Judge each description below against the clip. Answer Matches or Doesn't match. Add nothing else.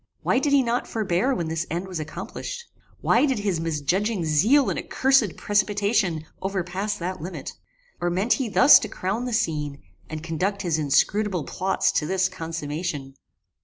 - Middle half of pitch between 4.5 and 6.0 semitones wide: Matches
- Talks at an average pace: Matches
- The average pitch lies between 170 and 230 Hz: Matches